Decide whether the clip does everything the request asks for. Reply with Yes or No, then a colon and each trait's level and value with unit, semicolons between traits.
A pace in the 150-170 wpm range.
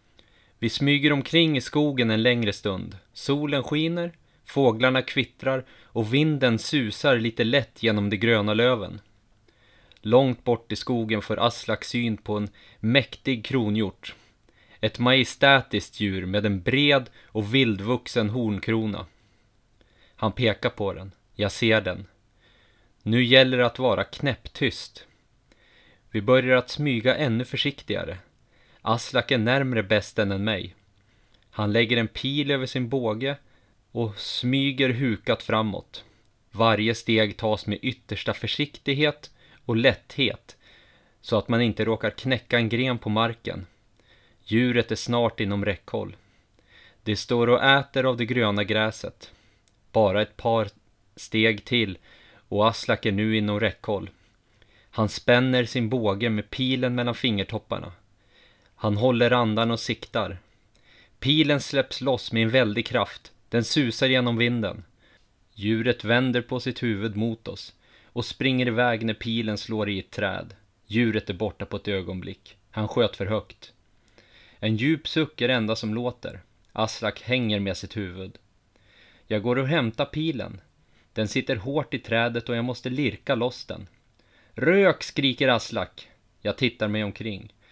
No: average, 140 wpm